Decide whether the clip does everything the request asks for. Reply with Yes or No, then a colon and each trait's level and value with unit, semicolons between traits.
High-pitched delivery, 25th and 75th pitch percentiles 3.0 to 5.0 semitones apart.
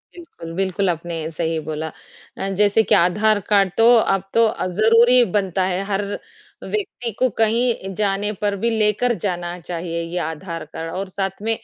Yes: high, 195 Hz; average, 3.9 semitones